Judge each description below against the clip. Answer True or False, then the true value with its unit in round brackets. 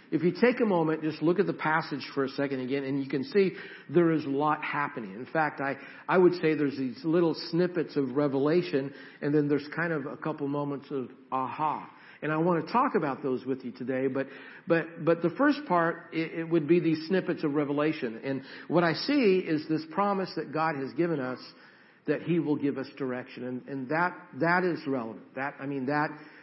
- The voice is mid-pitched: True (155 Hz)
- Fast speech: True (225 wpm)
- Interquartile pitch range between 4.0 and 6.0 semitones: False (3.4 semitones)